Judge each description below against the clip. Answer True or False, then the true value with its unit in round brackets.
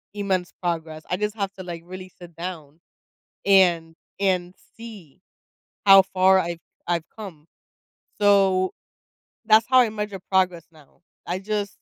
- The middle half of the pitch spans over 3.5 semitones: False (2.8 semitones)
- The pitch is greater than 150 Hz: True (185 Hz)